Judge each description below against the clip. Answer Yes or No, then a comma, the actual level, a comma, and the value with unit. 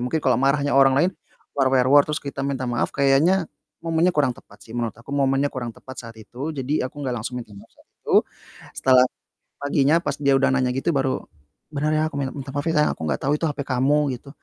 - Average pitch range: No, narrow, 1.9 semitones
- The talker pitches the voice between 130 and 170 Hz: Yes, low, 135 Hz